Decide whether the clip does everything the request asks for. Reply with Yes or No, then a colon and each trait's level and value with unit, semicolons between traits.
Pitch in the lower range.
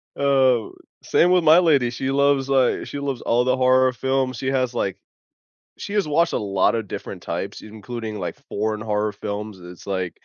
Yes: low, 125 Hz